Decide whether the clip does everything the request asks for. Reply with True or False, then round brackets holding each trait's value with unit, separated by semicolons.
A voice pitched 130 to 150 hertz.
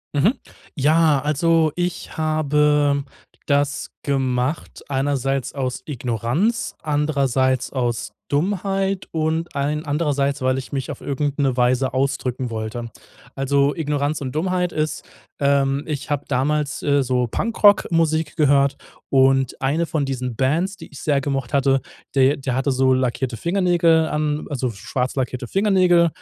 True (140 Hz)